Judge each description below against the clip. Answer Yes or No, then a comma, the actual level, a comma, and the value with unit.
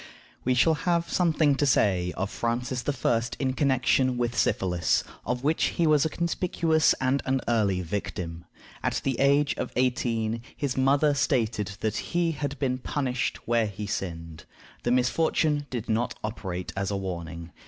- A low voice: Yes, low, 125 Hz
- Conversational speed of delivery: Yes, average, 160 wpm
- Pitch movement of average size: No, wide, 5.7 semitones